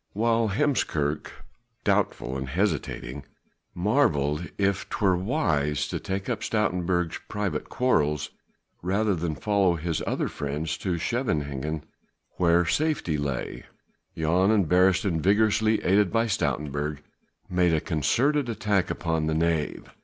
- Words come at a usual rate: No, slow, 120 wpm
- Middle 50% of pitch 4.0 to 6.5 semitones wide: Yes, wide, 5.4 semitones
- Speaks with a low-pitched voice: Yes, very low, 90 Hz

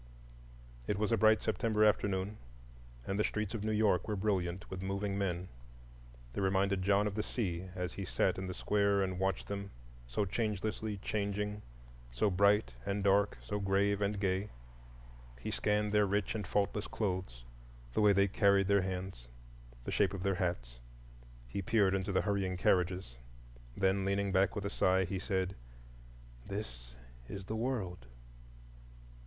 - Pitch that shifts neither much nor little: No, narrow, 1.8 semitones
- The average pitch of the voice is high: No, low, 100 Hz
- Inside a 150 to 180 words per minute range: Yes, average, 160 wpm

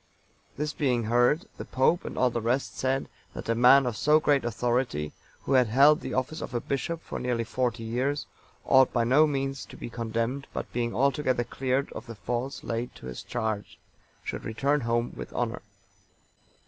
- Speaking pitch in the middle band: No, low, 125 Hz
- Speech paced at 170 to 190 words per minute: Yes, average, 185 wpm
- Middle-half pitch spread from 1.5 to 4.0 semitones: Yes, average, 2.8 semitones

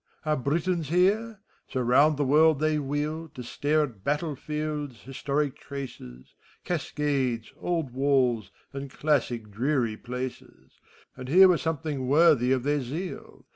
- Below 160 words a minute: Yes, slow, 135 wpm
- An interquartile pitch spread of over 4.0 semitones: No, average, 3.4 semitones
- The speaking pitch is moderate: Yes, medium, 145 Hz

